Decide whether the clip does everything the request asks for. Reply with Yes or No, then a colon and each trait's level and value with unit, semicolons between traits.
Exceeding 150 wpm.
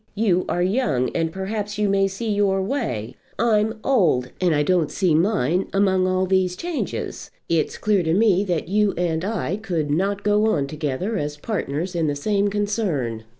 Yes: average, 180 wpm